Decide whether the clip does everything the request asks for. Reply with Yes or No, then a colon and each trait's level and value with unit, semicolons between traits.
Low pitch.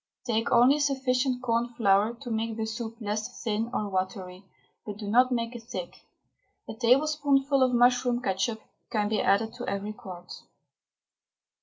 No: high, 230 Hz